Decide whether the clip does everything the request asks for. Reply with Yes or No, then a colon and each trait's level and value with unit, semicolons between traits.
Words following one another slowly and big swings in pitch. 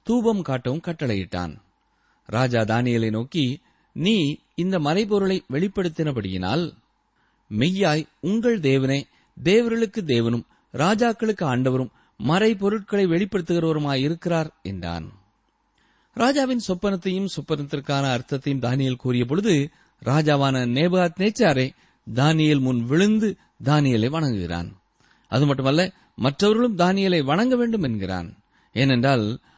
No: average, 85 wpm; wide, 7.2 semitones